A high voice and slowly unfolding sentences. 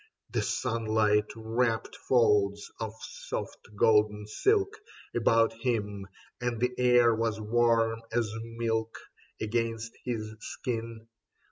No: low, 115 Hz; slow, 105 wpm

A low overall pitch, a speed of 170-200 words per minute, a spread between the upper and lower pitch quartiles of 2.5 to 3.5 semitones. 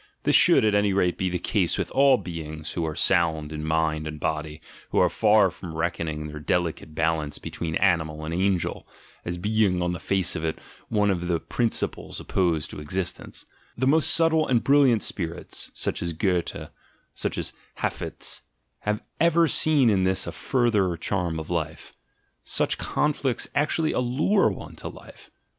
No: very low, 90 Hz; average, 180 wpm; average, 5.3 semitones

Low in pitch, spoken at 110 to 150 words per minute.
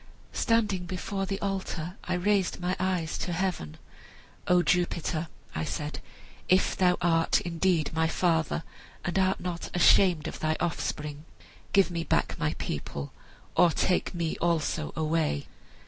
No: medium, 175 Hz; average, 140 wpm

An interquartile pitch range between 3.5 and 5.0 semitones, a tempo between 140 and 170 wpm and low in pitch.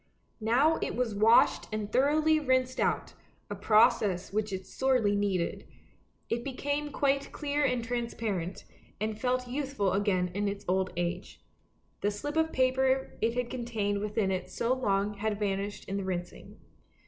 No: average, 4.4 semitones; average, 160 wpm; high, 220 Hz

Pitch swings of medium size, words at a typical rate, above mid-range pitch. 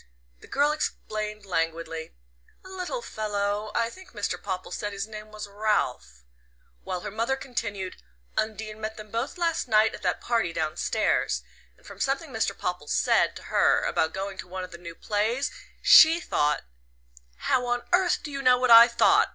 Yes: average, 4.6 semitones; average, 180 wpm; high, 215 Hz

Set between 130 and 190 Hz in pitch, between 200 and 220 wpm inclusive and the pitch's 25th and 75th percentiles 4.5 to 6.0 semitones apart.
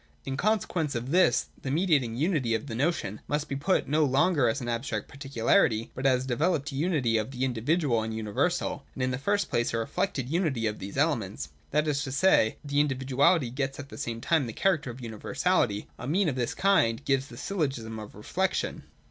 Yes: low, 135 Hz; fast, 205 wpm; average, 5.1 semitones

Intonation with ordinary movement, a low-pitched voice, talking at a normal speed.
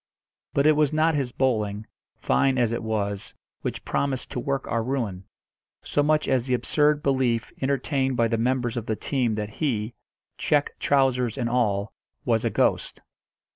Yes: average, 3.5 semitones; low, 125 Hz; average, 170 wpm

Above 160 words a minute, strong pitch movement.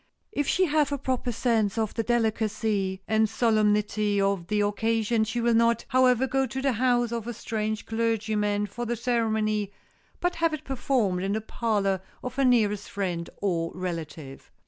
No: average, 170 wpm; average, 2.8 semitones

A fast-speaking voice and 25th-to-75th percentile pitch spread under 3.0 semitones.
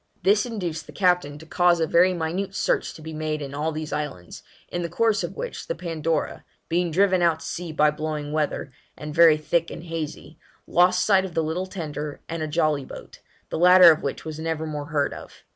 Yes: fast, 215 wpm; narrow, 2.6 semitones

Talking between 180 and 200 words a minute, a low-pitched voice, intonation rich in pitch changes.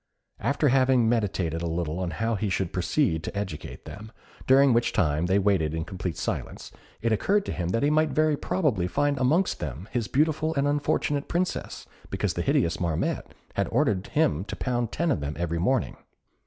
Yes: average, 195 wpm; low, 110 Hz; wide, 8.7 semitones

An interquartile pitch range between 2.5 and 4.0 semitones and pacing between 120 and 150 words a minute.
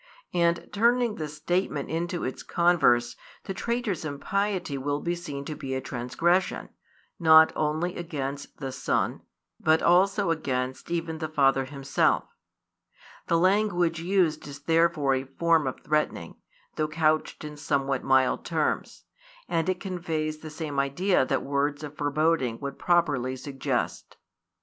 Yes: average, 3.7 semitones; average, 140 wpm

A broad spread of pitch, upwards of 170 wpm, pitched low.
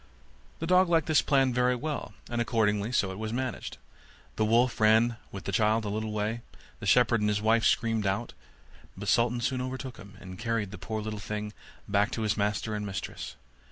No: narrow, 2.6 semitones; average, 200 wpm; low, 110 Hz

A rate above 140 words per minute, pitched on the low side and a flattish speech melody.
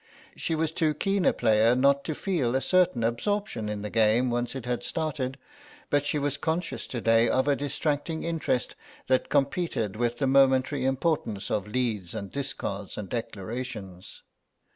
No: average, 165 wpm; low, 130 Hz; average, 4.7 semitones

